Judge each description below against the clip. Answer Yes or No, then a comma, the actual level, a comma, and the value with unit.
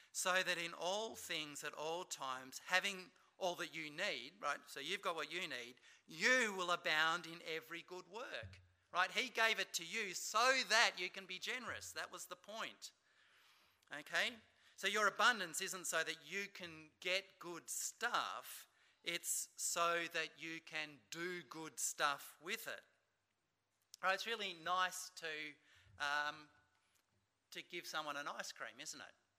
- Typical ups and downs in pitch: Yes, average, 3.1 semitones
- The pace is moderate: Yes, average, 160 wpm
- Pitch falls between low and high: Yes, medium, 170 Hz